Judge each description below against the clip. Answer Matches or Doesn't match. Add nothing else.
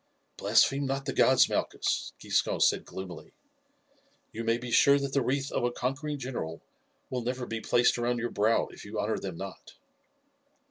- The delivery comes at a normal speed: Matches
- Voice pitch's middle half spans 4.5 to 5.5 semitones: Doesn't match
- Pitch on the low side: Matches